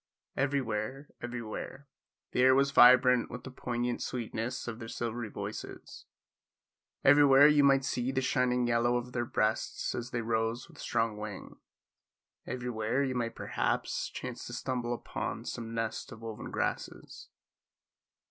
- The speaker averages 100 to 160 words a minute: Yes, average, 140 wpm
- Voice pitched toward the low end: Yes, low, 120 Hz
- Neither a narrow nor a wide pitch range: No, narrow, 2.2 semitones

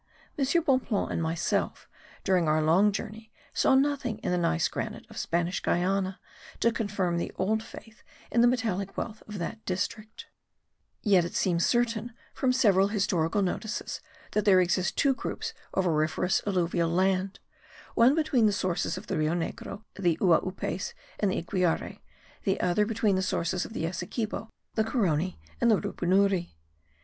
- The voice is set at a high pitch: Yes, high, 195 Hz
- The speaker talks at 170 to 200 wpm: No, average, 160 wpm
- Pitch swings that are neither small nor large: Yes, average, 3.9 semitones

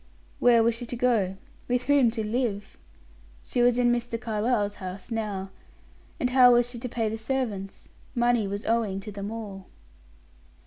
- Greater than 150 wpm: Yes, average, 170 wpm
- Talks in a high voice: Yes, high, 230 Hz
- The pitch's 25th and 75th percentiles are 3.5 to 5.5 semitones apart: No, average, 2.9 semitones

